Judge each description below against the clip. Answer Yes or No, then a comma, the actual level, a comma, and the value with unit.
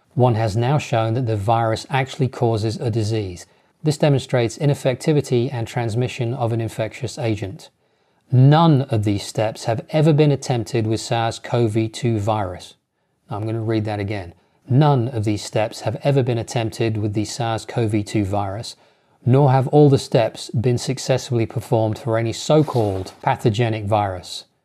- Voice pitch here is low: Yes, low, 115 Hz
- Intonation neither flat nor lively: Yes, average, 3.2 semitones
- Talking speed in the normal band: Yes, average, 165 wpm